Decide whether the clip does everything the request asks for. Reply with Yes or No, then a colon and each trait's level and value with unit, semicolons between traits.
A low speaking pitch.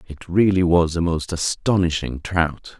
Yes: very low, 85 Hz